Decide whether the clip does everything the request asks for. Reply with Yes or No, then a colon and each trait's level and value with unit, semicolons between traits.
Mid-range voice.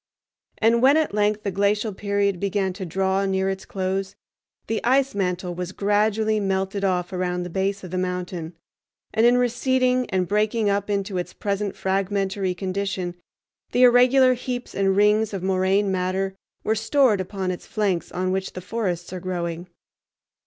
No: high, 195 Hz